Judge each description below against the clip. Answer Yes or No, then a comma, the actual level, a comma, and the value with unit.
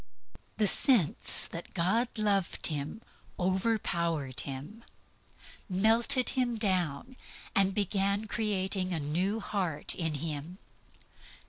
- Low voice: No, high, 190 Hz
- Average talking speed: No, slow, 110 wpm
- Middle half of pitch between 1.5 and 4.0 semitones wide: No, average, 4.5 semitones